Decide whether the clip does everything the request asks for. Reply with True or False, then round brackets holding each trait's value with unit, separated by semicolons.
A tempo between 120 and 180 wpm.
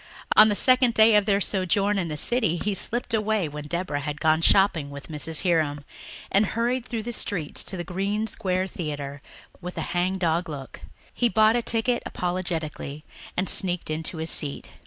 False (190 wpm)